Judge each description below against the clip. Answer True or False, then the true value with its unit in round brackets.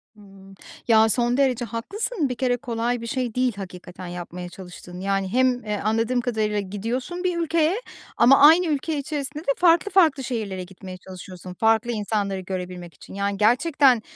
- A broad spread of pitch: True (5.7 semitones)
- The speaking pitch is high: True (230 Hz)